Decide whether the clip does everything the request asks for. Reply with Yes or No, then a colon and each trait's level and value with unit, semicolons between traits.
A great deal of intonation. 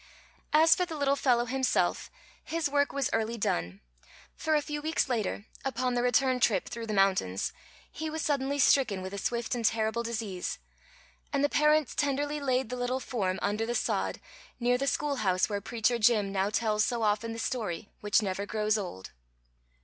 No: average, 4.8 semitones